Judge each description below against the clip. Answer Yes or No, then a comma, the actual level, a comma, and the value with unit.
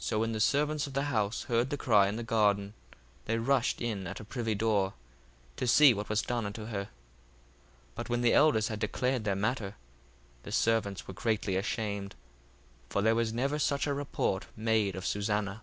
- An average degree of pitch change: Yes, average, 3.1 semitones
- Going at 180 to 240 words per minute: Yes, average, 200 wpm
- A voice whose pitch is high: No, low, 110 Hz